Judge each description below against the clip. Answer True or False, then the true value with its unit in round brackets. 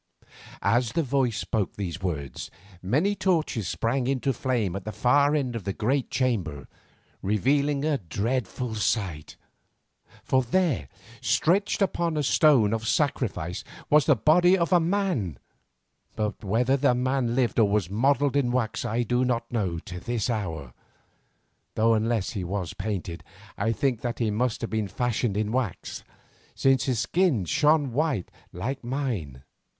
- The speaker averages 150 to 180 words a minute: True (155 wpm)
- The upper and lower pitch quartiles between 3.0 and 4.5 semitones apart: False (5.1 semitones)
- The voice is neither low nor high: False (120 Hz)